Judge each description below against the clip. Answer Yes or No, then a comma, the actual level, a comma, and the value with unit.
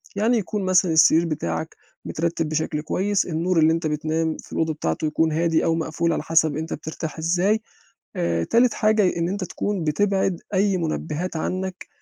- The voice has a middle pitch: Yes, medium, 165 Hz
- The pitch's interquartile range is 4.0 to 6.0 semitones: No, average, 3.0 semitones